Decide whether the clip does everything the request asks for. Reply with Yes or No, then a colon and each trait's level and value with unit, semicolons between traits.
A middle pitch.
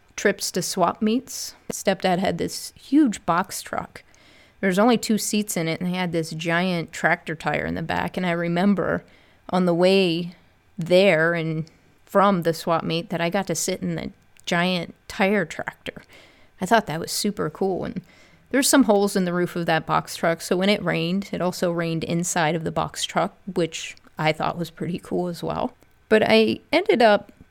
Yes: medium, 180 Hz